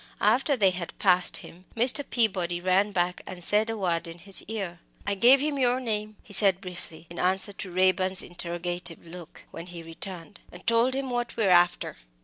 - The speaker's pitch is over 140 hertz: Yes, high, 190 Hz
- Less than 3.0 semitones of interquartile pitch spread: No, average, 4.0 semitones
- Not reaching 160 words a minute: No, average, 195 wpm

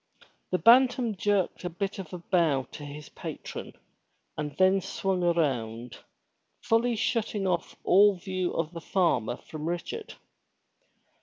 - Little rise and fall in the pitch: No, average, 4.4 semitones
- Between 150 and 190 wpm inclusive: No, average, 140 wpm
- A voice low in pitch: No, medium, 180 Hz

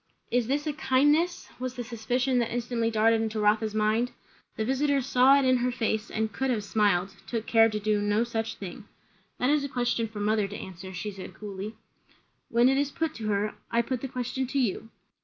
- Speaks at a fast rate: Yes, fast, 215 wpm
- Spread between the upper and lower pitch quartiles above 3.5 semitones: No, average, 3.2 semitones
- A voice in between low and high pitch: No, high, 230 Hz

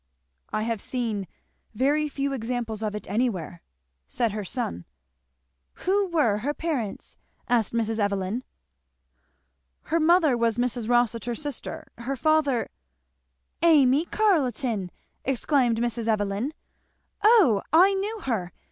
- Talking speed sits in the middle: No, slow, 120 wpm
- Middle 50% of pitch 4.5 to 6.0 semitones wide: Yes, wide, 5.4 semitones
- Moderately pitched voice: No, high, 240 Hz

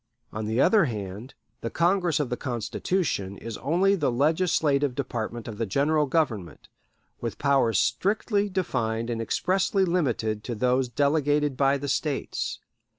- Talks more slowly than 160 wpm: Yes, average, 145 wpm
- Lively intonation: Yes, wide, 5.8 semitones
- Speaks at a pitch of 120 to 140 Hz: Yes, low, 135 Hz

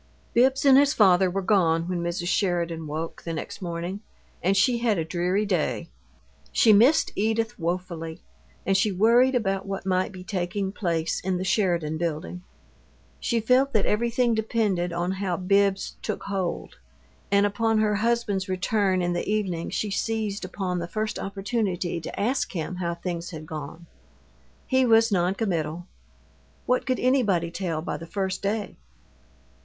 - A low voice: No, high, 190 Hz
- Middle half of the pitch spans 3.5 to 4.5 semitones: Yes, average, 3.9 semitones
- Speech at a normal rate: Yes, average, 160 wpm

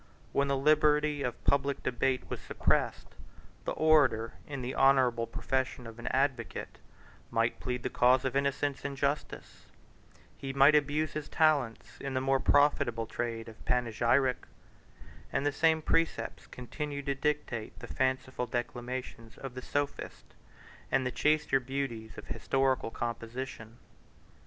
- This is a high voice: No, low, 135 Hz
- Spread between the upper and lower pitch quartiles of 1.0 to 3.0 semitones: Yes, narrow, 2.6 semitones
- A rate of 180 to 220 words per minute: No, average, 140 wpm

